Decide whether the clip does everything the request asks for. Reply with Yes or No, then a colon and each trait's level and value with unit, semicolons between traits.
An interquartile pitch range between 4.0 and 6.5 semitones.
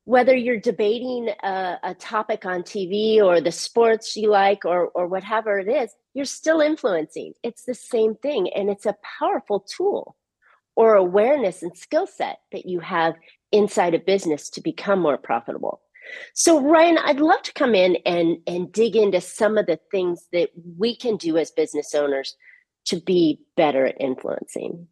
Yes: wide, 5.5 semitones